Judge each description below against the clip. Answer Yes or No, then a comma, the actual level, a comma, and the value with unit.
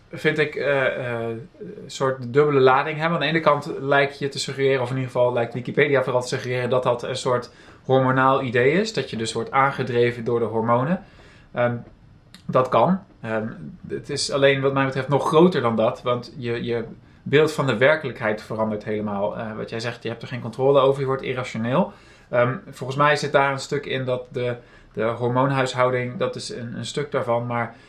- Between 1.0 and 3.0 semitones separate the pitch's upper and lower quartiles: Yes, average, 2.7 semitones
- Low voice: Yes, low, 130 Hz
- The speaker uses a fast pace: Yes, fast, 205 wpm